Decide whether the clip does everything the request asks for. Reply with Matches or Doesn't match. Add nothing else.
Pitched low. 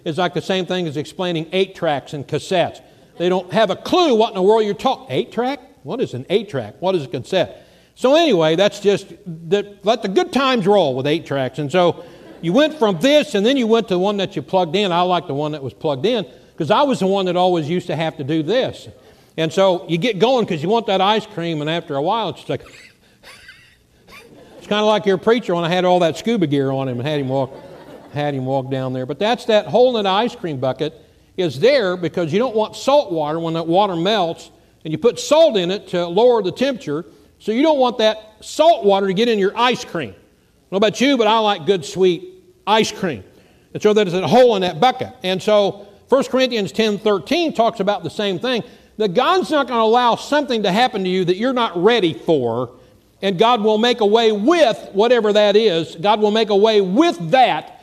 Doesn't match